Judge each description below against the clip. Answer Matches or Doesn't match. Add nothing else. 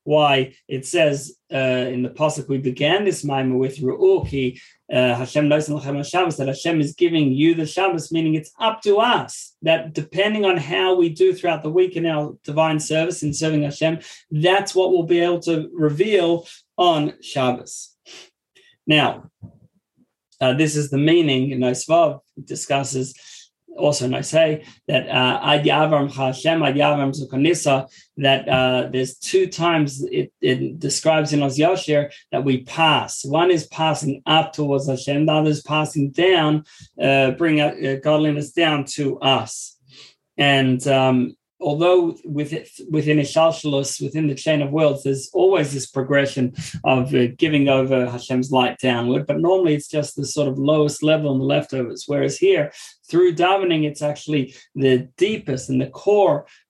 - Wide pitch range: Doesn't match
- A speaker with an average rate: Matches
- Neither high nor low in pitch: Matches